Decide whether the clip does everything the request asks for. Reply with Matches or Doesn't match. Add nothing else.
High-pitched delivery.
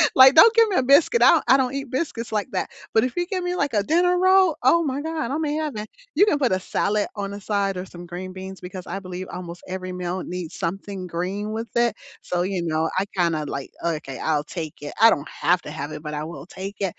Matches